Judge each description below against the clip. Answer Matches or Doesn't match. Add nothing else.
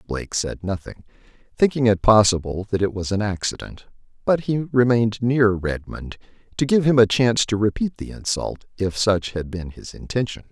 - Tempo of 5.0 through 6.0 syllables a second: Matches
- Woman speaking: Doesn't match